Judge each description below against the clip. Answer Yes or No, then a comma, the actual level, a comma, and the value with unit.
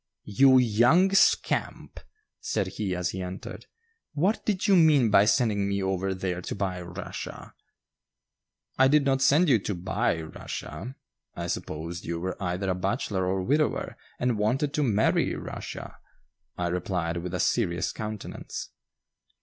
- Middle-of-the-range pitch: No, low, 100 Hz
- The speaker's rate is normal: Yes, average, 150 wpm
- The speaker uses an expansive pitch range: Yes, wide, 6.5 semitones